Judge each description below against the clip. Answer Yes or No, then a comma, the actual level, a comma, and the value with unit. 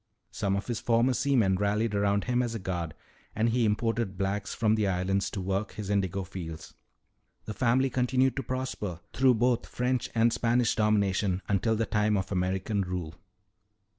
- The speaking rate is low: No, average, 170 wpm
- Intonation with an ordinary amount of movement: Yes, average, 3.5 semitones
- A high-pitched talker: No, low, 105 Hz